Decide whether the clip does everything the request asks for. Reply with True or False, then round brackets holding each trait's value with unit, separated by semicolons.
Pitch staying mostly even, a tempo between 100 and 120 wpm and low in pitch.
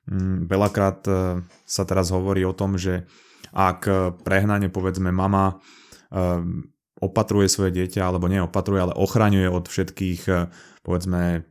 True (1.2 semitones; 110 wpm; 95 Hz)